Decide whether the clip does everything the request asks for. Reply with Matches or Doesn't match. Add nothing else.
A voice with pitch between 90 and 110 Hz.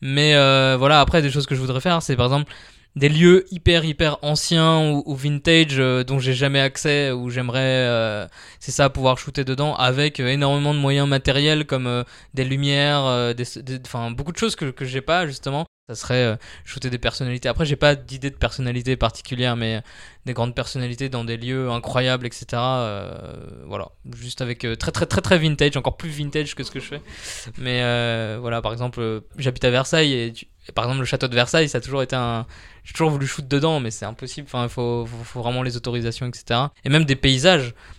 Doesn't match